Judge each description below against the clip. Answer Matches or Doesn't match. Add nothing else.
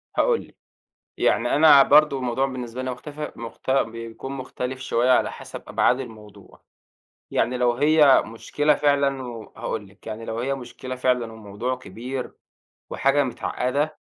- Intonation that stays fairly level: Doesn't match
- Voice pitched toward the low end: Matches